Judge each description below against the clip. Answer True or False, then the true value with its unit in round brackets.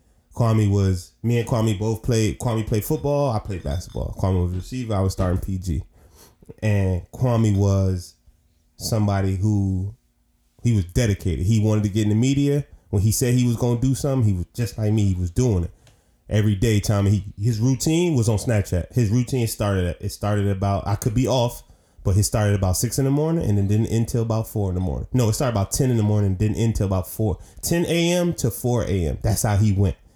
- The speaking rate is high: True (225 wpm)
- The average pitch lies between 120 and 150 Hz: False (105 Hz)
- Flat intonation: False (3.9 semitones)